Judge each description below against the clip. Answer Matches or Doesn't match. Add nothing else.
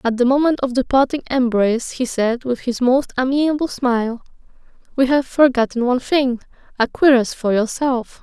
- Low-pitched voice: Doesn't match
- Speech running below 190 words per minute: Matches